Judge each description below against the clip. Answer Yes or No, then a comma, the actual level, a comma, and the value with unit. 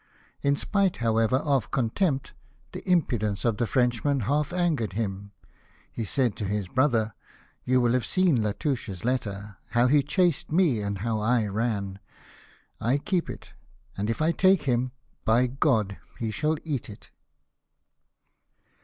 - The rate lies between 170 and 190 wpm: No, average, 150 wpm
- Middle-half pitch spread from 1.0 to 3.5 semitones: No, average, 5.0 semitones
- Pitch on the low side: Yes, low, 120 Hz